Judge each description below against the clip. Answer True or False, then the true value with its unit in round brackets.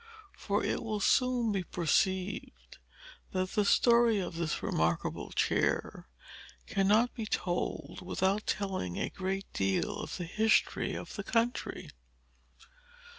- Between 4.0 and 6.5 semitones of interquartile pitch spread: False (3.3 semitones)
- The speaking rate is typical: False (125 wpm)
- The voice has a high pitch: True (195 Hz)